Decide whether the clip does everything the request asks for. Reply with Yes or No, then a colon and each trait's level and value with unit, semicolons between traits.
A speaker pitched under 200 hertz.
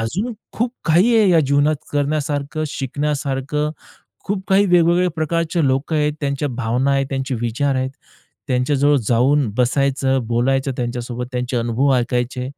Yes: medium, 140 Hz